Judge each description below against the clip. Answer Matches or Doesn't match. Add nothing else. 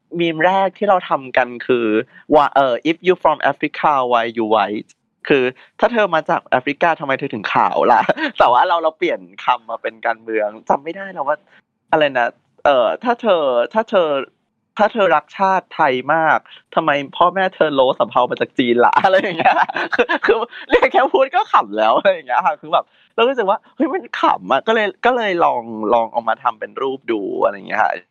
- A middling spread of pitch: Doesn't match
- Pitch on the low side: Doesn't match